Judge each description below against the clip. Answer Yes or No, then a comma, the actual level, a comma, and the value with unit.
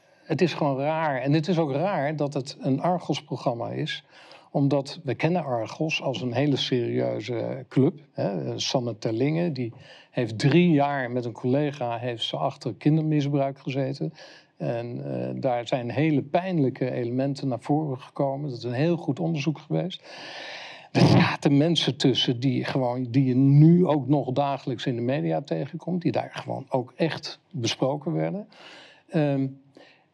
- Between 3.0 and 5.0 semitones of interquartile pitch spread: Yes, average, 3.3 semitones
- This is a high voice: No, medium, 140 Hz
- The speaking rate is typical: Yes, average, 160 wpm